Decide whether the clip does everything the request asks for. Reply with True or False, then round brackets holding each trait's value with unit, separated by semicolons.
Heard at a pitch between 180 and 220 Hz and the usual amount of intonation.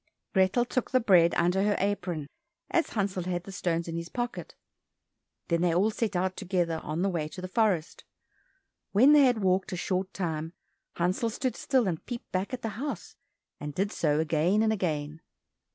True (185 Hz; 4.3 semitones)